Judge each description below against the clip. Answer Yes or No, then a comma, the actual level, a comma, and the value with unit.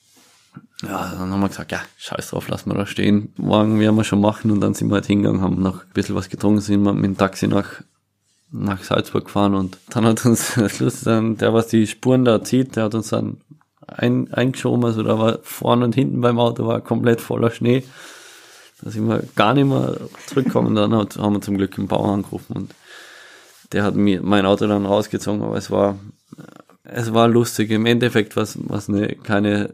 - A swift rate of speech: Yes, fast, 205 wpm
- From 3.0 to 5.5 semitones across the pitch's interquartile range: No, narrow, 2.5 semitones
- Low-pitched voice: Yes, low, 105 Hz